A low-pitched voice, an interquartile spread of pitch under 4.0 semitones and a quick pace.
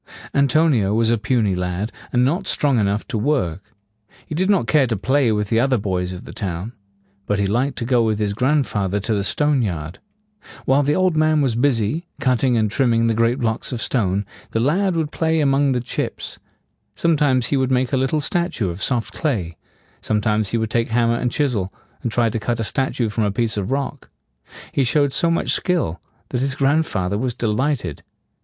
No: low, 120 Hz; average, 4.9 semitones; fast, 210 wpm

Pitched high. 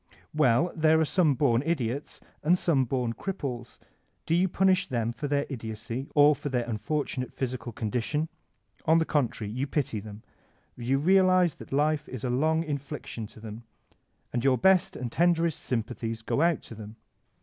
No: low, 135 Hz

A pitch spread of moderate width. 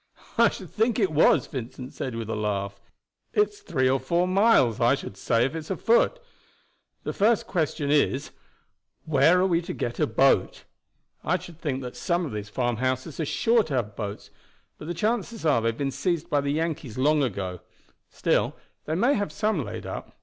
No: wide, 6.7 semitones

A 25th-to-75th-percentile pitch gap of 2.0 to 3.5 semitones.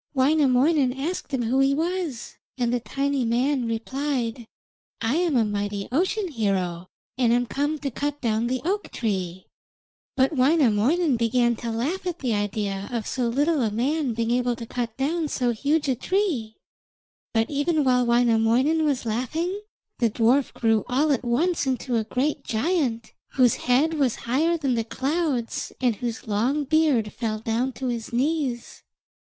No: average, 4.2 semitones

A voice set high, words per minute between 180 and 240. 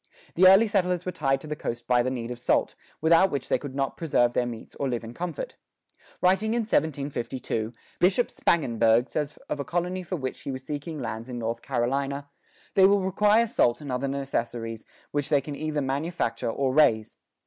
No: medium, 140 Hz; average, 195 wpm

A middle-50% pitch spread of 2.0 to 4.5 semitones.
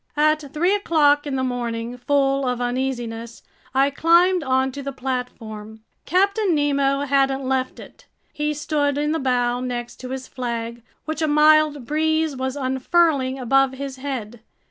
Yes: average, 3.1 semitones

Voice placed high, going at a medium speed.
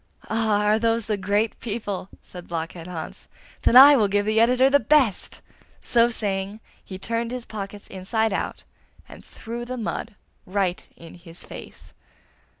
Yes: high, 215 Hz; average, 155 wpm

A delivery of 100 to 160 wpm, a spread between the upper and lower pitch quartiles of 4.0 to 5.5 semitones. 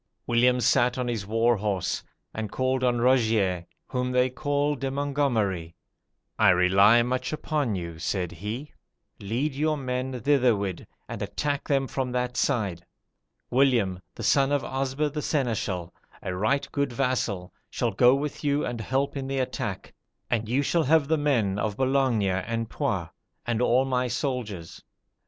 Yes: average, 155 wpm; average, 4.6 semitones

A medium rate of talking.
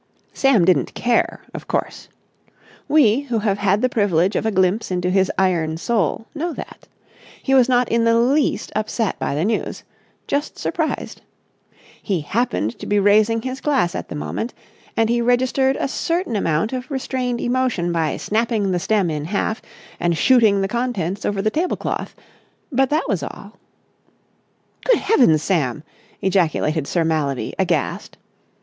Yes: average, 160 wpm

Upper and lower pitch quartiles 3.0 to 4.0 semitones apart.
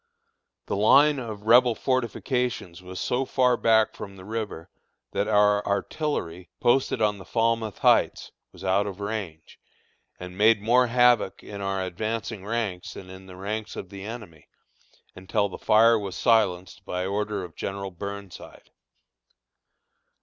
Yes: average, 3.3 semitones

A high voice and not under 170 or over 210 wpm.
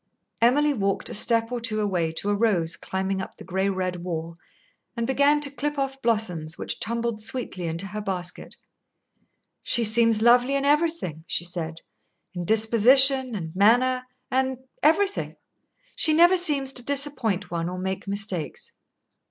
No: high, 225 Hz; average, 155 wpm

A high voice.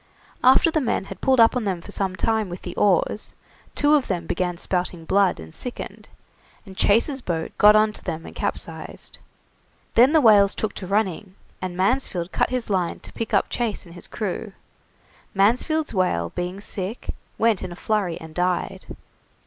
Yes: high, 200 Hz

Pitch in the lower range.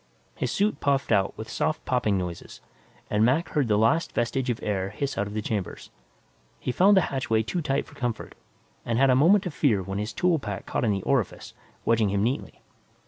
Yes: low, 120 Hz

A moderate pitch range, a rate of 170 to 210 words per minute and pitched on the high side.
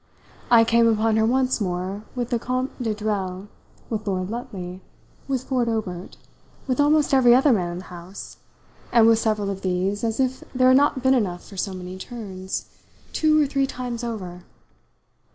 Yes: average, 5.0 semitones; average, 180 wpm; high, 225 Hz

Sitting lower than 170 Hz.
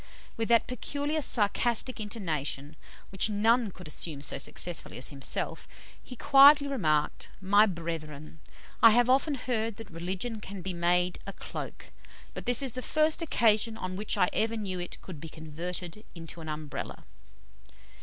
No: high, 200 Hz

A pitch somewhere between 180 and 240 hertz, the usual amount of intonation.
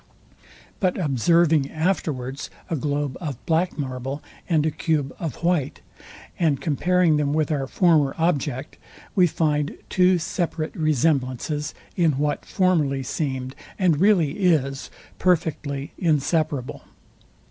No: medium, 155 Hz; average, 3.5 semitones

